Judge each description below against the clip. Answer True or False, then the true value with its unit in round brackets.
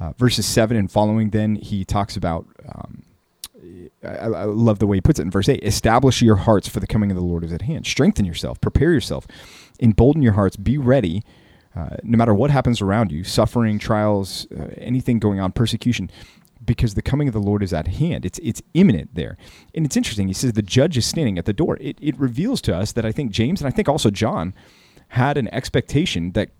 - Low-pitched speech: True (110 Hz)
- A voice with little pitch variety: False (3.4 semitones)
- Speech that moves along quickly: True (225 wpm)